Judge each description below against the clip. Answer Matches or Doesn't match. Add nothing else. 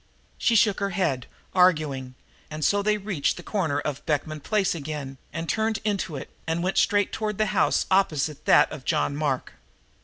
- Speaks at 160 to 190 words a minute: Matches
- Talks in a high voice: Doesn't match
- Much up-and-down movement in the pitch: Matches